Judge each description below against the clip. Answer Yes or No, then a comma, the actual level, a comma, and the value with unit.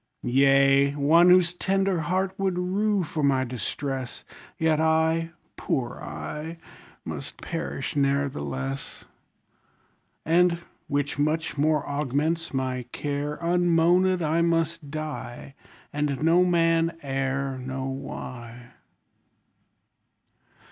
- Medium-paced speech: No, slow, 100 wpm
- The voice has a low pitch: No, medium, 150 Hz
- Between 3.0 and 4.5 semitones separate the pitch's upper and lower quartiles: Yes, average, 3.6 semitones